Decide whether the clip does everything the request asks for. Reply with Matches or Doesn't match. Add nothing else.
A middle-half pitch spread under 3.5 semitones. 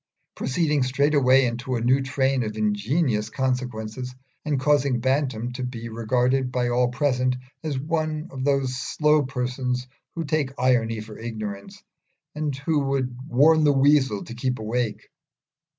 Matches